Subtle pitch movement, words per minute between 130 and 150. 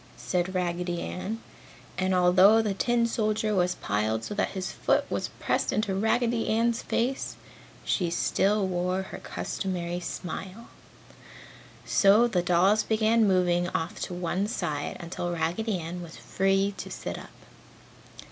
No: average, 3.4 semitones; average, 140 wpm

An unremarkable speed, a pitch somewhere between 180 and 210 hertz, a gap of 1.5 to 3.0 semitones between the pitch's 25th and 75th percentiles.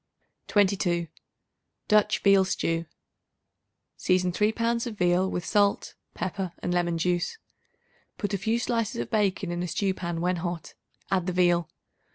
Yes: average, 150 wpm; medium, 185 Hz; average, 2.7 semitones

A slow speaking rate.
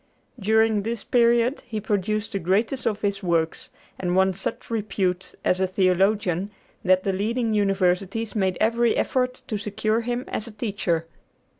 No: average, 155 wpm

